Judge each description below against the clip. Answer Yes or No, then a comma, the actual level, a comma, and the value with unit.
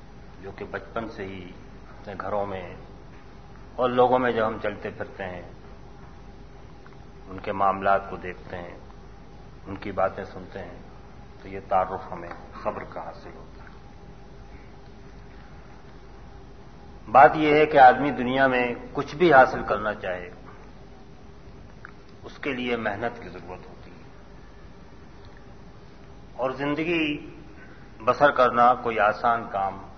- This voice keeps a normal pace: No, slow, 125 wpm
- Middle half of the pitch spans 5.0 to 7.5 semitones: No, average, 4.6 semitones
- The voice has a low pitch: Yes, low, 105 Hz